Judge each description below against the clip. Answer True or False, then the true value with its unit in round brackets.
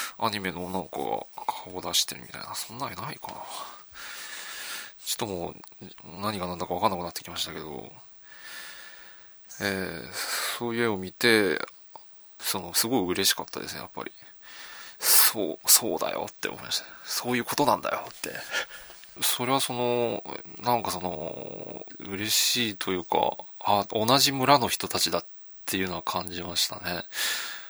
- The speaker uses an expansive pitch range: False (4.8 semitones)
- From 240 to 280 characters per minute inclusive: False (305 characters per minute)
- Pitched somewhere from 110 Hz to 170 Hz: False (100 Hz)